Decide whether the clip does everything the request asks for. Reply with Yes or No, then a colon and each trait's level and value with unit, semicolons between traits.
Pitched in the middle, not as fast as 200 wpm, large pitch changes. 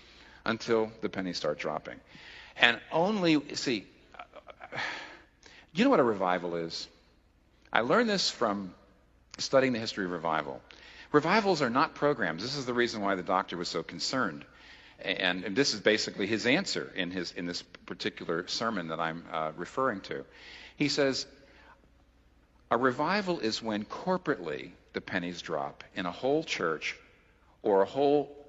No: low, 110 Hz; average, 150 wpm; wide, 8.0 semitones